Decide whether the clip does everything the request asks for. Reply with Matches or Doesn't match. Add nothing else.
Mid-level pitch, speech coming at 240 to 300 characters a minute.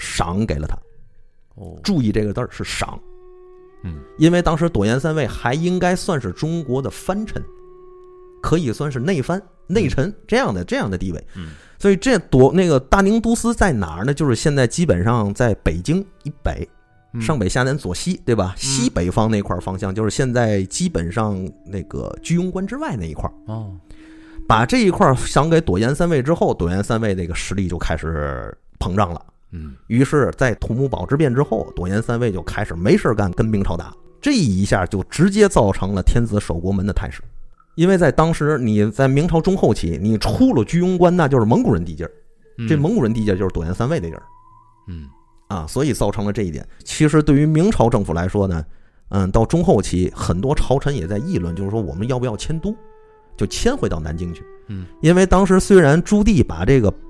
Doesn't match